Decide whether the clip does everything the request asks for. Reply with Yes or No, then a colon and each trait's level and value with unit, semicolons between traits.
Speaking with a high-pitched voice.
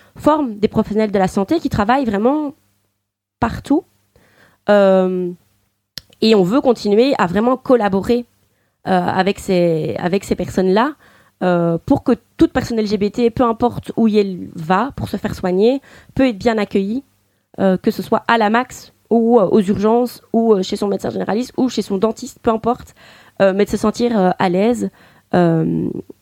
Yes: high, 215 Hz